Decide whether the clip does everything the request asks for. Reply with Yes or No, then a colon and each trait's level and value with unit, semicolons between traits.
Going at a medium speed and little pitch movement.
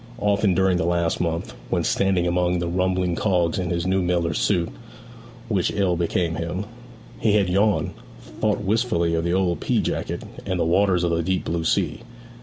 Yes: average, 185 wpm; narrow, 2.0 semitones